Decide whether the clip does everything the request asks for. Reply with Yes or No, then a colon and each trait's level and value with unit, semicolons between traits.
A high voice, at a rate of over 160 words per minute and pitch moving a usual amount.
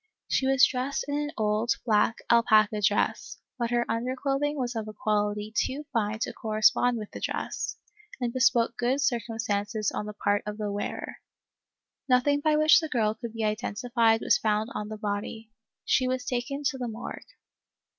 Yes: high, 230 Hz; average, 175 wpm; average, 3.2 semitones